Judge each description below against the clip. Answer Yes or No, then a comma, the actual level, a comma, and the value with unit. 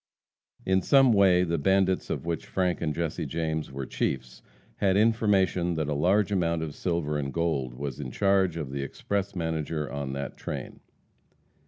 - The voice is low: Yes, very low, 85 Hz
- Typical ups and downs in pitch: Yes, average, 4.6 semitones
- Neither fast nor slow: Yes, average, 170 wpm